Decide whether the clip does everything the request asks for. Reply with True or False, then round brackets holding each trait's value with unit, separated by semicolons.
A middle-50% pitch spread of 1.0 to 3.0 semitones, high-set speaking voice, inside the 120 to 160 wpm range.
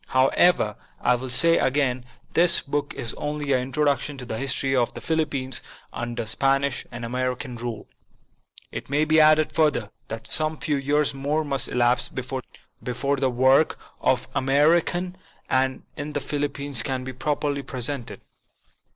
False (2.7 semitones; 135 Hz; 145 wpm)